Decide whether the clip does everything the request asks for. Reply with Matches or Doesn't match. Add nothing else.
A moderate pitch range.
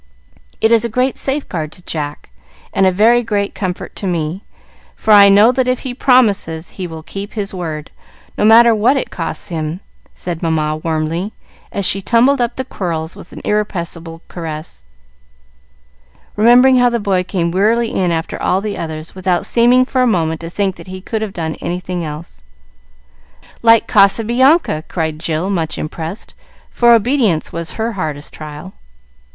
Doesn't match